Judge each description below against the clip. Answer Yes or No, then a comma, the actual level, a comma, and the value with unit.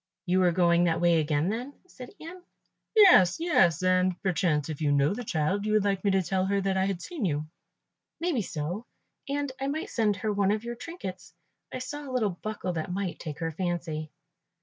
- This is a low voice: No, high, 190 Hz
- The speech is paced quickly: Yes, fast, 215 wpm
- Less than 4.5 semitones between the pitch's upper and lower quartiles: No, average, 5.1 semitones